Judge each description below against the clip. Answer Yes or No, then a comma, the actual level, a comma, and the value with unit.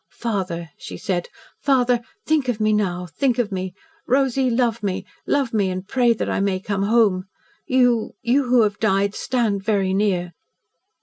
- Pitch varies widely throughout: No, average, 4.3 semitones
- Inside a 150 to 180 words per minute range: Yes, average, 170 wpm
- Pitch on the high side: Yes, high, 215 Hz